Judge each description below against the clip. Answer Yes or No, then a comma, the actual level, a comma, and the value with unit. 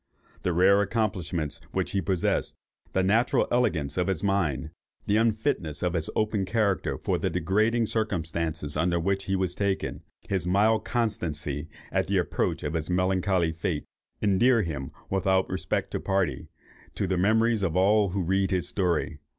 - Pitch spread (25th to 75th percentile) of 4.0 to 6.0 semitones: No, average, 3.5 semitones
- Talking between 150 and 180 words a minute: Yes, average, 165 wpm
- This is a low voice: Yes, very low, 95 Hz